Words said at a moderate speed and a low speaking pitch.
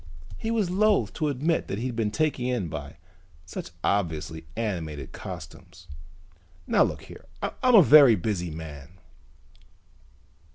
No: slow, 130 wpm; low, 105 Hz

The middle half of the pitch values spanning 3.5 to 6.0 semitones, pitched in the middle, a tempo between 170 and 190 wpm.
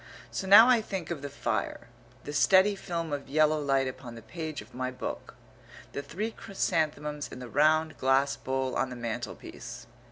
Yes: average, 4.1 semitones; medium, 145 Hz; average, 180 wpm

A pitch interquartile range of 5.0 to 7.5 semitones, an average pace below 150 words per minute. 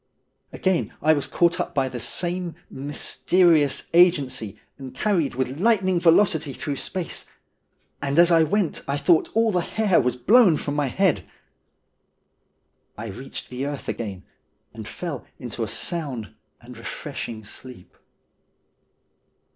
Yes: average, 5.3 semitones; average, 140 wpm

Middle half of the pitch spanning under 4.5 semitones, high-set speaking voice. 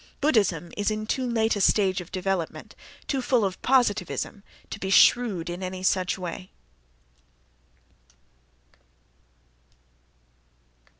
Yes: average, 3.5 semitones; high, 195 Hz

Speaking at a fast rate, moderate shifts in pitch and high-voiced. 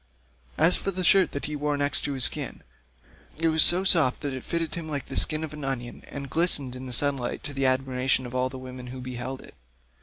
No: fast, 240 wpm; average, 3.4 semitones; medium, 140 Hz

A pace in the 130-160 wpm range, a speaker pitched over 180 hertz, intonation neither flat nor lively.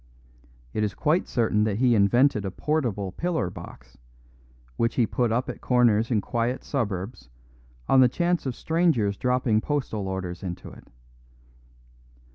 No: average, 145 wpm; low, 115 Hz; average, 4.6 semitones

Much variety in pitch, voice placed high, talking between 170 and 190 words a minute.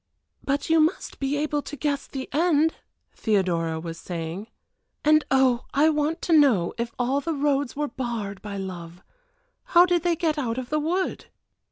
Yes: wide, 6.7 semitones; very high, 275 Hz; average, 175 wpm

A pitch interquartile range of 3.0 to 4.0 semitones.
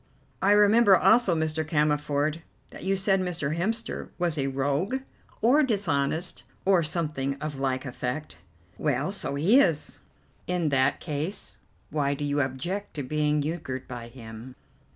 No: average, 5.0 semitones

